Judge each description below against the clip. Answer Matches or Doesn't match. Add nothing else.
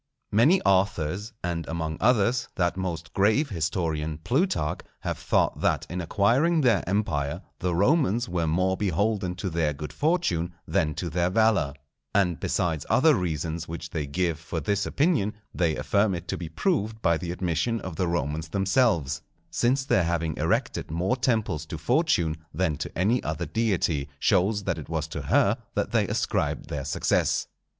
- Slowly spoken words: Doesn't match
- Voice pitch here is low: Matches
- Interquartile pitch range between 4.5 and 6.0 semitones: Matches